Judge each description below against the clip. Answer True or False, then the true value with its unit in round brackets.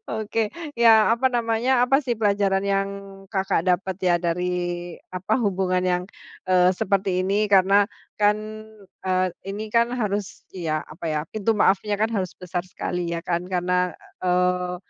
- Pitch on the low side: False (190 Hz)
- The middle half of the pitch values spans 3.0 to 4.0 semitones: False (2.4 semitones)